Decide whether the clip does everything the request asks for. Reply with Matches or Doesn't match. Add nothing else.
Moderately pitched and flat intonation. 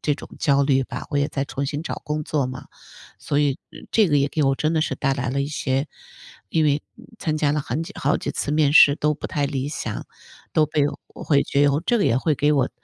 Matches